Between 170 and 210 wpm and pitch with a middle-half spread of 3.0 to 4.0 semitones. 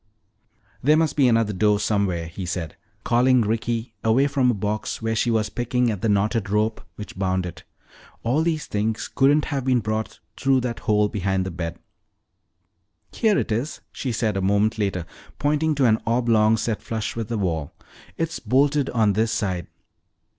Yes: average, 175 wpm; average, 3.6 semitones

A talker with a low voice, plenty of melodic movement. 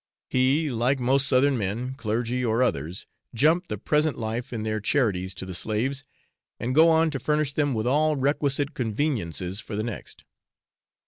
No: low, 125 Hz; average, 4.6 semitones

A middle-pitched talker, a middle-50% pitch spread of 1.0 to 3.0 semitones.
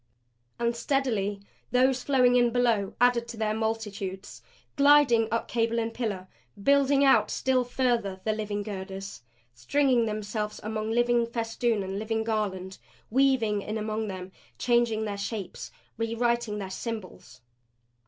No: high, 225 Hz; average, 2.7 semitones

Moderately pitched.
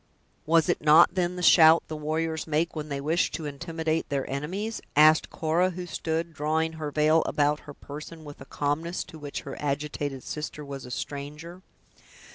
Yes: medium, 155 Hz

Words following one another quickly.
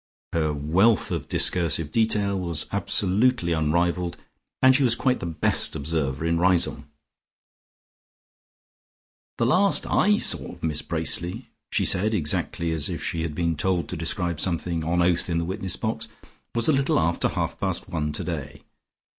No: average, 155 wpm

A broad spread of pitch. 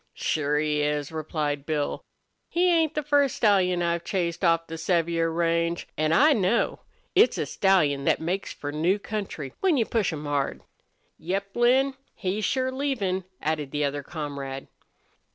Yes: wide, 6.0 semitones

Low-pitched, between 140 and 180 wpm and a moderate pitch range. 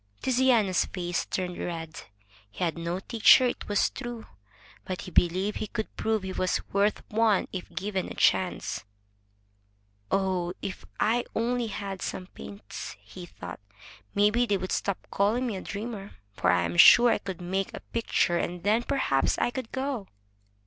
No: high, 200 Hz; average, 165 wpm; average, 3.9 semitones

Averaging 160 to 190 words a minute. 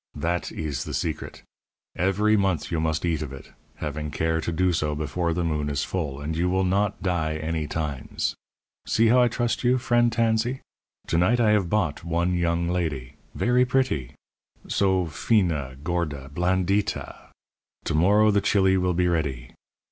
Yes: average, 170 wpm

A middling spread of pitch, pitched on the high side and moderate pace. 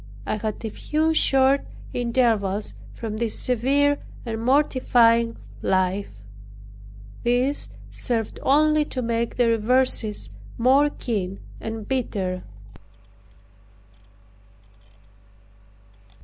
No: average, 3.4 semitones; high, 235 Hz; slow, 85 wpm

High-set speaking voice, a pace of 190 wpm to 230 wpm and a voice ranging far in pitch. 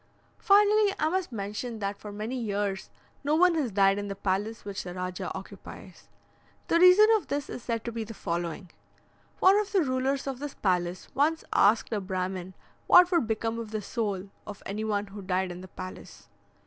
Yes: high, 215 Hz; average, 195 wpm; wide, 6.4 semitones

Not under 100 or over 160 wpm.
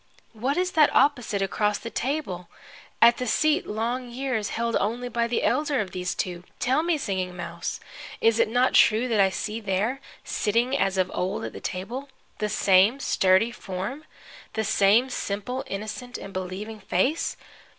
No: average, 170 wpm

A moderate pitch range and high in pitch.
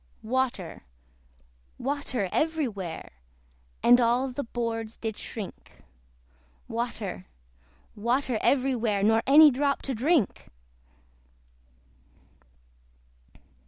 Yes: average, 3.8 semitones; high, 240 Hz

